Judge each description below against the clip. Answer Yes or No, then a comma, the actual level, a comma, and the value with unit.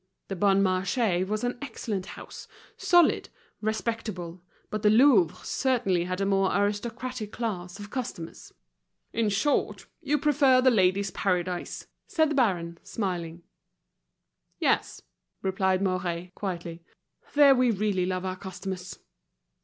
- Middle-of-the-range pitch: No, high, 195 Hz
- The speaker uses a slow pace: Yes, slow, 125 wpm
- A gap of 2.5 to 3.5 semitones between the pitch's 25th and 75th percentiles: No, average, 4.1 semitones